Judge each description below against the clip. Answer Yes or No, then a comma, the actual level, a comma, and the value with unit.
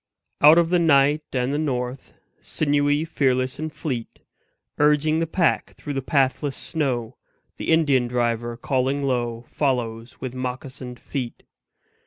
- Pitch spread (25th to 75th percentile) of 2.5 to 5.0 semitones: Yes, average, 3.2 semitones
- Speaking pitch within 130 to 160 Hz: Yes, low, 135 Hz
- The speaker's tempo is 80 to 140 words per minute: Yes, slow, 135 wpm